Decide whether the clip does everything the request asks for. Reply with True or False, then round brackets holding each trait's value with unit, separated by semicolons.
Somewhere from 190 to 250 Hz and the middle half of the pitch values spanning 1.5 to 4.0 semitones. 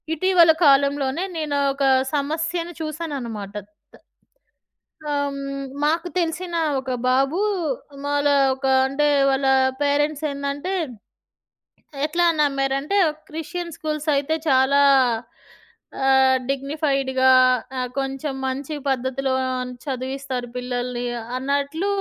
False (280 Hz; 2.5 semitones)